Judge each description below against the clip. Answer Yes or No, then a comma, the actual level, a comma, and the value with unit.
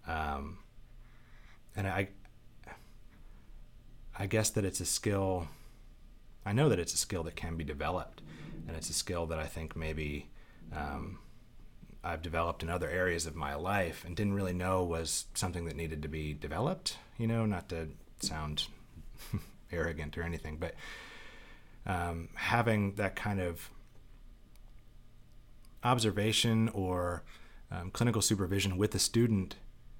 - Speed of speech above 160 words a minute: No, average, 140 wpm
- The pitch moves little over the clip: No, wide, 5.5 semitones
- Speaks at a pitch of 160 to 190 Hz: No, very low, 95 Hz